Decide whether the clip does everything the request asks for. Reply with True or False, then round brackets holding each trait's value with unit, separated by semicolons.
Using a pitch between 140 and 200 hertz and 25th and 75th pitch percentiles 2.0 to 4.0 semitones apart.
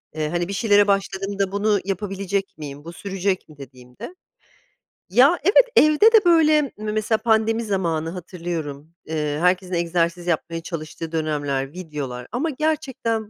False (185 Hz; 5.3 semitones)